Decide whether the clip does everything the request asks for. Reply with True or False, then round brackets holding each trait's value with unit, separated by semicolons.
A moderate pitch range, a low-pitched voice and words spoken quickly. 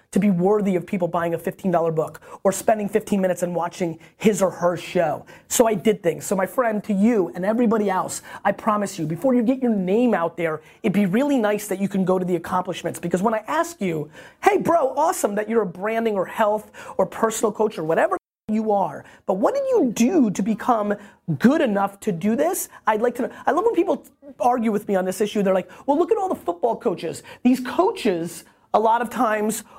False (4.9 semitones; 210 Hz; 230 wpm)